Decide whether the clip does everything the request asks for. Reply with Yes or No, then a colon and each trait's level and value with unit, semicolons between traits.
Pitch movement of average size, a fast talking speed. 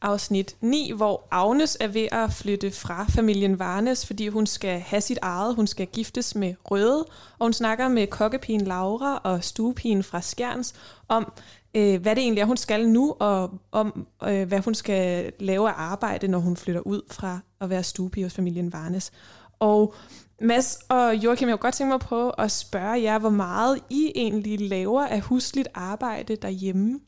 No: average, 3.5 semitones; average, 180 wpm